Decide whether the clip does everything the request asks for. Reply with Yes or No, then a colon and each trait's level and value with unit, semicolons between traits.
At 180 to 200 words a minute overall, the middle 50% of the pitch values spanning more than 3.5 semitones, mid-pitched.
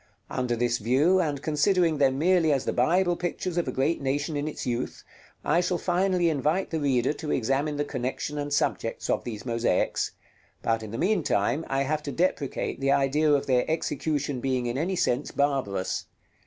Yes: average, 185 wpm; average, 4.1 semitones; medium, 145 Hz